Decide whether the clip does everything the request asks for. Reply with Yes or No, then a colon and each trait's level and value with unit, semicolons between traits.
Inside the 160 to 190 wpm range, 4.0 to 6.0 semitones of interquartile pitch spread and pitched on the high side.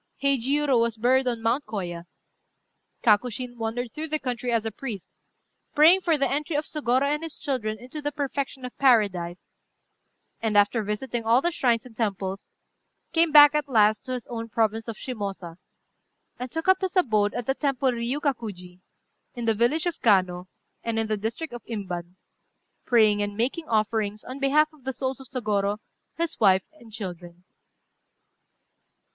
Yes: average, 165 wpm; average, 4.6 semitones; high, 235 Hz